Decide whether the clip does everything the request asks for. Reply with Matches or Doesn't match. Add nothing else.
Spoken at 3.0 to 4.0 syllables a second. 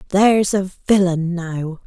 Matches